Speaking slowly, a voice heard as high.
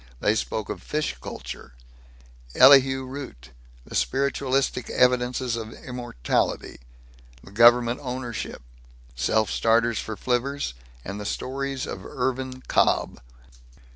No: slow, 105 wpm; low, 125 Hz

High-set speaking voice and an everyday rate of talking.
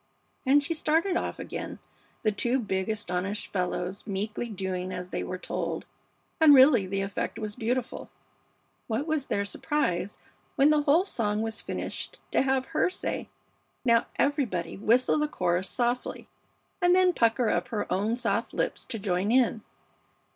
Yes: high, 225 Hz; average, 155 wpm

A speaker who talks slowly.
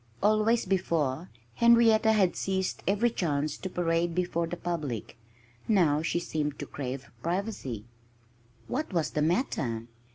Yes: slow, 130 wpm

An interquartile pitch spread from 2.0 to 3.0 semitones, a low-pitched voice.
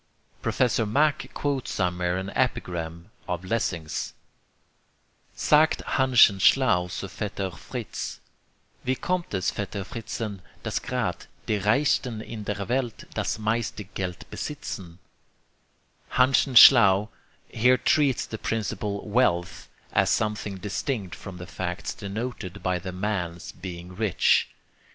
No: average, 4.9 semitones; low, 105 Hz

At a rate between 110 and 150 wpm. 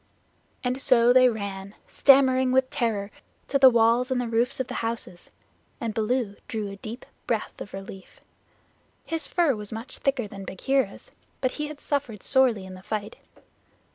No: average, 170 wpm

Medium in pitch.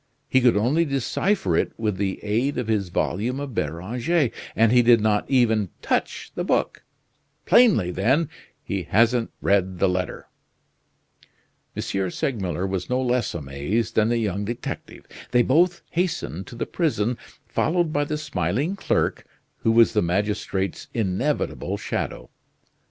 No: low, 115 Hz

